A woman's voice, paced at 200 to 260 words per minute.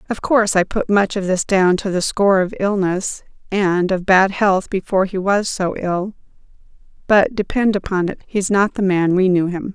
Yes: female; fast, 205 wpm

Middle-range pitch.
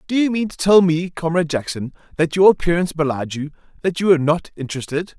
Yes: medium, 165 Hz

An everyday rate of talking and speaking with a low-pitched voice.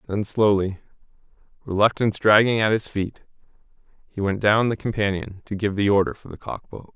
Yes: average, 170 wpm; low, 105 Hz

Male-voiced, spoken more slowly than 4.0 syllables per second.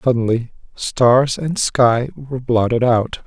Yes: male; 3.8 syllables/s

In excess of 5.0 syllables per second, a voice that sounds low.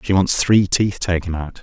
No: 4.6 syllables/s; very low, 90 Hz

